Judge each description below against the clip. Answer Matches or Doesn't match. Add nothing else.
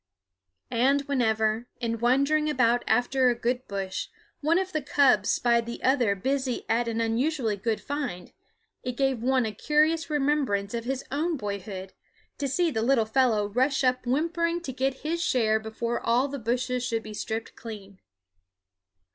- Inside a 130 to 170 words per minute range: Matches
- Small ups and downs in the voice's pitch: Doesn't match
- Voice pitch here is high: Matches